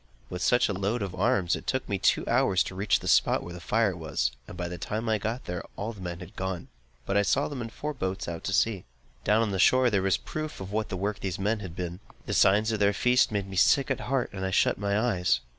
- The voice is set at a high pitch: No, low, 100 Hz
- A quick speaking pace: Yes, fast, 280 wpm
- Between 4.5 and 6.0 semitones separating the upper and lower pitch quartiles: No, average, 3.4 semitones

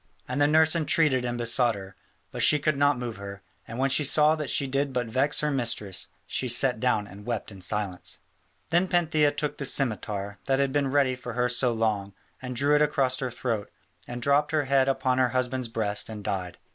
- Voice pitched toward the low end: Yes, low, 130 Hz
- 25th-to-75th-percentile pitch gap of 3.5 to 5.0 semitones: Yes, average, 4.2 semitones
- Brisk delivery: Yes, fast, 215 wpm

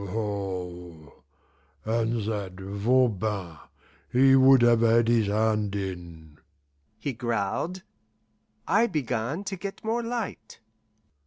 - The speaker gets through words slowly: Yes, slow, 100 wpm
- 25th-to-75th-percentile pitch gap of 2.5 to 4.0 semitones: No, average, 5.0 semitones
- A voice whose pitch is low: Yes, low, 110 Hz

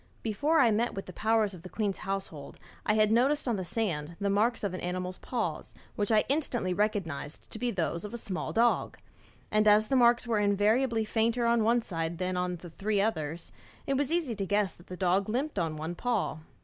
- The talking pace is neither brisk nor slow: No, fast, 215 wpm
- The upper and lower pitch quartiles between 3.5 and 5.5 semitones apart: Yes, average, 4.3 semitones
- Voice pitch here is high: Yes, high, 210 Hz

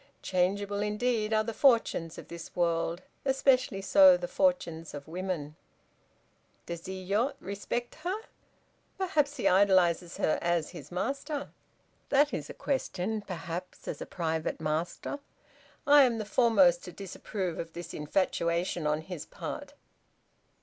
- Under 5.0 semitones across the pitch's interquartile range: No, wide, 5.5 semitones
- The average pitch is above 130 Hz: Yes, high, 190 Hz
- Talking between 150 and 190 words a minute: No, slow, 135 wpm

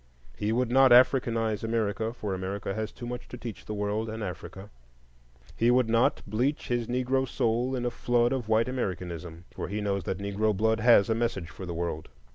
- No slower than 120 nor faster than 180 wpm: No, average, 200 wpm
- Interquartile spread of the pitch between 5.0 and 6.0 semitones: No, average, 3.3 semitones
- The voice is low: Yes, low, 110 Hz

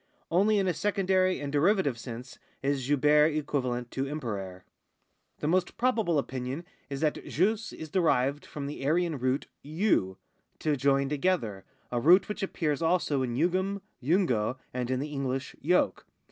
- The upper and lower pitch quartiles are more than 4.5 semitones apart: Yes, wide, 5.6 semitones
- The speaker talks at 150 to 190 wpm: Yes, average, 155 wpm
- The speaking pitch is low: No, medium, 145 Hz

